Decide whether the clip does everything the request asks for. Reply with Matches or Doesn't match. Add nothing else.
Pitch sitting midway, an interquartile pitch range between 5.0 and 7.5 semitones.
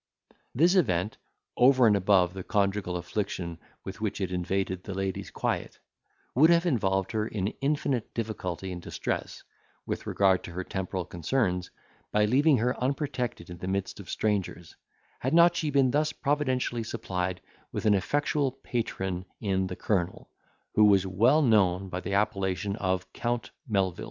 Doesn't match